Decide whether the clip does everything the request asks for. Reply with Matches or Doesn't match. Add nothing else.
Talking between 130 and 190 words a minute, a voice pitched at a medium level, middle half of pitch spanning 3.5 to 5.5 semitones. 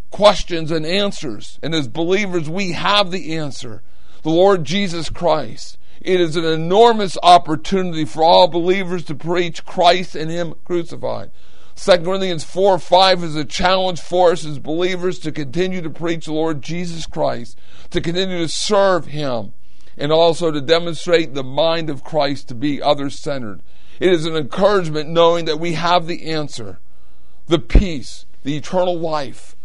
Doesn't match